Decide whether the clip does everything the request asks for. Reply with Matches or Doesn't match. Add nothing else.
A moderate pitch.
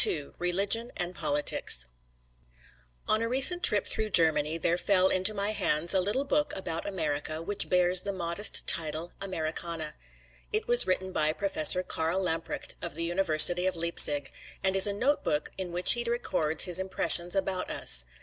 Matches